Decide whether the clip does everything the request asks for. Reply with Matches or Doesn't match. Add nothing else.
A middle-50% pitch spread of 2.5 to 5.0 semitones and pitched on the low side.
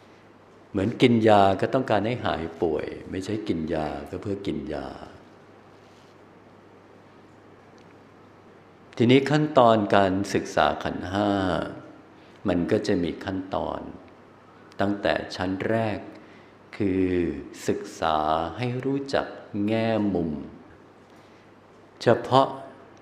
Matches